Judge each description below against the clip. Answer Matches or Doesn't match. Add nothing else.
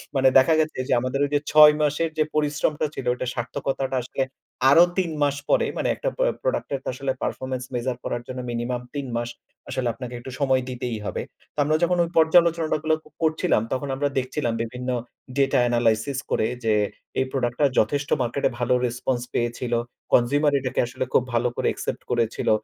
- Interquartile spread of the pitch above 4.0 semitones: Doesn't match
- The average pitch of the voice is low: Matches